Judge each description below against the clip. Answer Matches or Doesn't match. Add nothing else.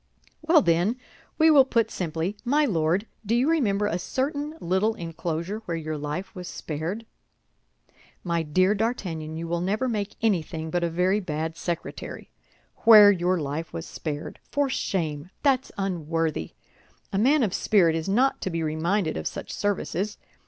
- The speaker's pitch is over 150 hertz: Matches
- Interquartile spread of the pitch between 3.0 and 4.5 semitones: Doesn't match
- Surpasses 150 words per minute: Matches